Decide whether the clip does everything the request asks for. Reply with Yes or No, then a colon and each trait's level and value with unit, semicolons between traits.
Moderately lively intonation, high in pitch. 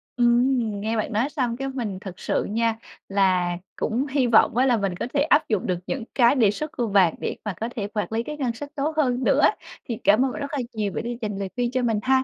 Yes: average, 4.0 semitones; high, 235 Hz